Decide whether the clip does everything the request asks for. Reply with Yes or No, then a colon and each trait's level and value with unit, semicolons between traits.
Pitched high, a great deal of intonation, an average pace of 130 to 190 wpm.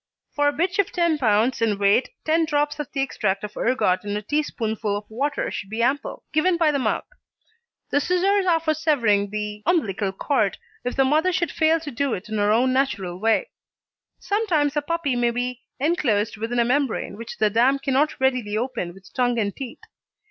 No: very high, 255 Hz; wide, 5.9 semitones; average, 200 wpm